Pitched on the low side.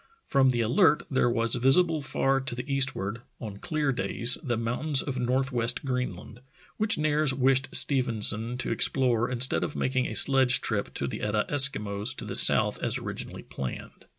Yes: low, 125 Hz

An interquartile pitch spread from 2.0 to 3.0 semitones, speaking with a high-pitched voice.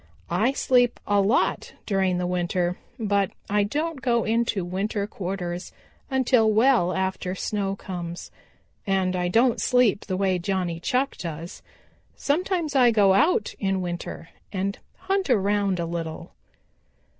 No: average, 4.6 semitones; high, 200 Hz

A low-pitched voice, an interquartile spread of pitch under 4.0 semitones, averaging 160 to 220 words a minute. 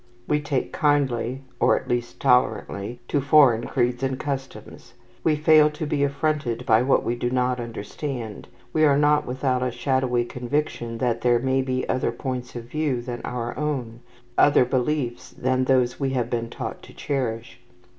Yes: low, 130 Hz; average, 2.8 semitones; average, 170 wpm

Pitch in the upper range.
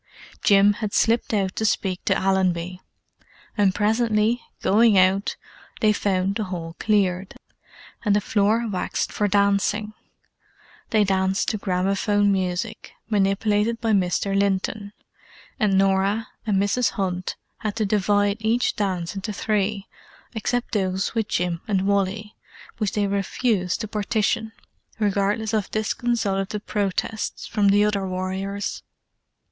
Yes: high, 200 Hz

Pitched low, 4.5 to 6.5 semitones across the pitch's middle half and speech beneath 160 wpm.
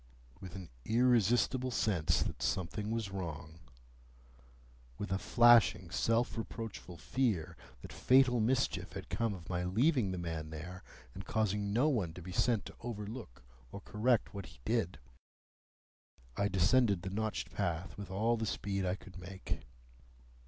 Yes: very low, 95 Hz; average, 5.2 semitones; average, 145 wpm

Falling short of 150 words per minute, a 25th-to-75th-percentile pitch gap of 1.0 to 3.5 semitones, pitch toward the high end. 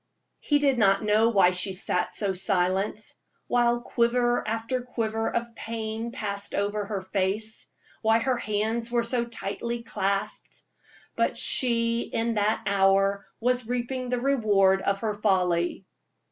Yes: average, 140 wpm; average, 3.1 semitones; high, 220 Hz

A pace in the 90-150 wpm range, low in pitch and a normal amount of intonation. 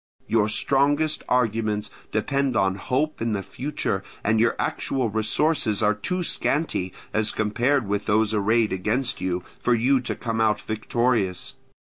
Yes: average, 145 wpm; low, 110 Hz; average, 3.8 semitones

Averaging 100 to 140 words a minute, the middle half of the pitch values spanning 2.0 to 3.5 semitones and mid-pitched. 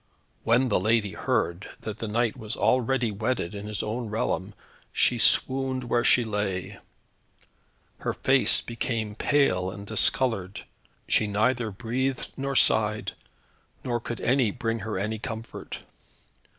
No: slow, 135 wpm; average, 2.8 semitones; low, 110 Hz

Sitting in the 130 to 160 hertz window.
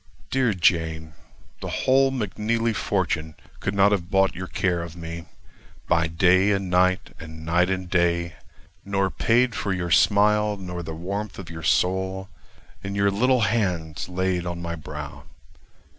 No: very low, 95 Hz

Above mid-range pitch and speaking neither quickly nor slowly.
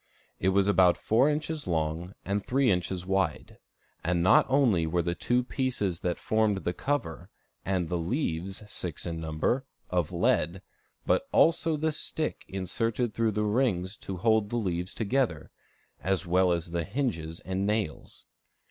No: very low, 95 Hz; average, 155 wpm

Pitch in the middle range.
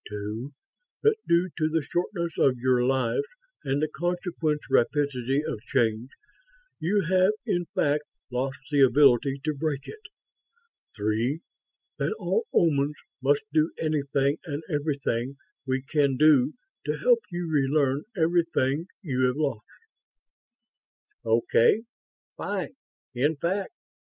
Yes: medium, 145 Hz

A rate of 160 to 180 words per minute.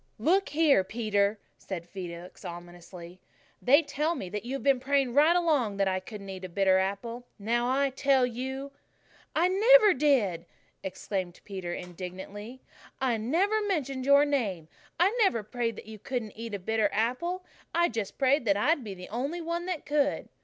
Yes: average, 175 wpm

